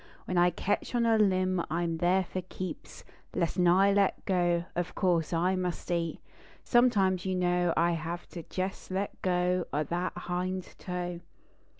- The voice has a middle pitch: Yes, medium, 180 Hz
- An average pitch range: No, narrow, 1.4 semitones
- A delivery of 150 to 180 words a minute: Yes, average, 170 wpm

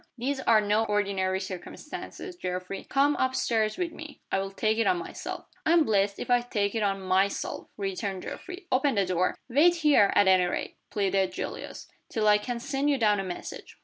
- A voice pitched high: Yes, high, 215 Hz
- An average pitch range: No, wide, 5.8 semitones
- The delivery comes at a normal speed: Yes, average, 190 wpm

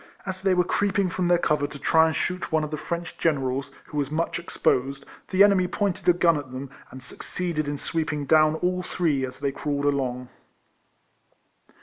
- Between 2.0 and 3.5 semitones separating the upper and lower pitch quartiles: No, average, 4.0 semitones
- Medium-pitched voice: Yes, medium, 155 Hz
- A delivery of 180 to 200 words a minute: Yes, average, 195 wpm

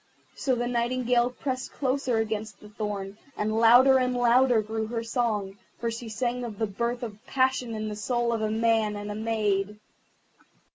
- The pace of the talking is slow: No, average, 180 wpm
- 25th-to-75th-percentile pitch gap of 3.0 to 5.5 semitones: No, narrow, 2.4 semitones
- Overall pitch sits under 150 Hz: No, high, 230 Hz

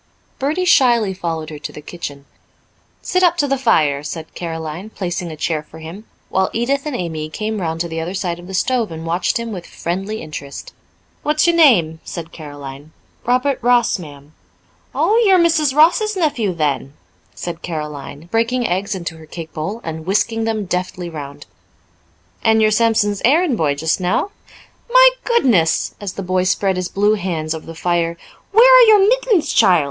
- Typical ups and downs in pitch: No, wide, 7.3 semitones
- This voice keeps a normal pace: Yes, average, 180 wpm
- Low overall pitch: No, medium, 185 Hz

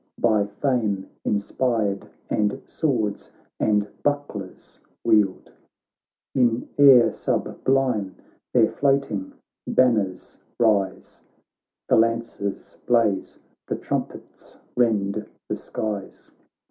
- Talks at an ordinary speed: No, slow, 85 wpm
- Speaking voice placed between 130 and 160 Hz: No, low, 110 Hz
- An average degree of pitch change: Yes, average, 3.5 semitones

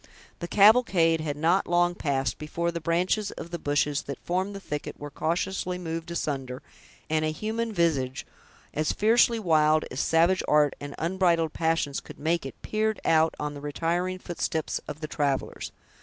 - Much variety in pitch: No, average, 3.4 semitones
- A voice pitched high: No, medium, 165 Hz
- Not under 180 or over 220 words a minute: No, average, 170 wpm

